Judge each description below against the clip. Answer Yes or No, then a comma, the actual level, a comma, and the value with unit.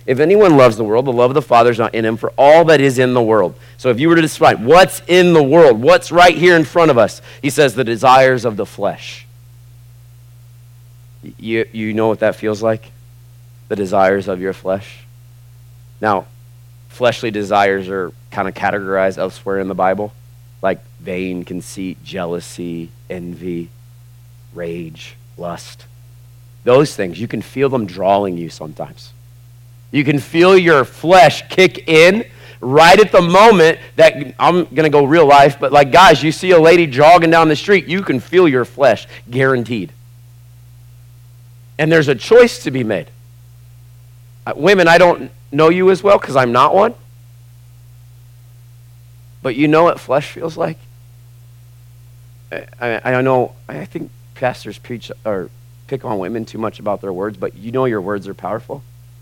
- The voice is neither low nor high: No, low, 120 Hz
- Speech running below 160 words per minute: No, average, 170 wpm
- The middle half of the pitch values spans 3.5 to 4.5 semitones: No, average, 3.0 semitones